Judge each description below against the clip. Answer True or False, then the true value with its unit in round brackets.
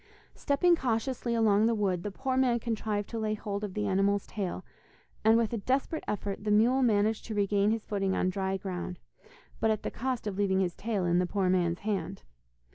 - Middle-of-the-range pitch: False (210 Hz)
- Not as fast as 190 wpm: False (205 wpm)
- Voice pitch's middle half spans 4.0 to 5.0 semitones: False (2.9 semitones)